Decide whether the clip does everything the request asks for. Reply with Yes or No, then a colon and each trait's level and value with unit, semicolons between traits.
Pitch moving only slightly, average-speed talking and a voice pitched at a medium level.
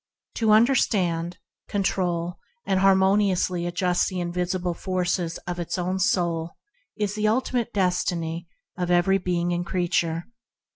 No: narrow, 1.8 semitones; slow, 125 wpm; medium, 180 Hz